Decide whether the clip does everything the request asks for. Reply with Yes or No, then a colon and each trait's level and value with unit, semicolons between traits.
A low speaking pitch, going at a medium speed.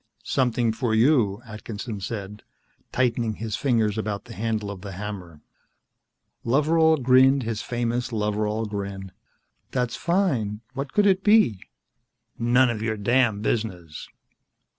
No: low, 115 Hz; slow, 125 wpm